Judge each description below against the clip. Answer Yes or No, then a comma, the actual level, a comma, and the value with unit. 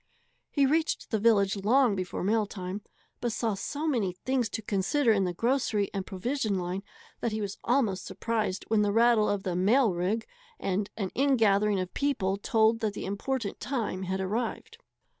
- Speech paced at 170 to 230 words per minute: Yes, average, 180 wpm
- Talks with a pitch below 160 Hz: No, high, 215 Hz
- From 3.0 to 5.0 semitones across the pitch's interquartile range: Yes, average, 3.7 semitones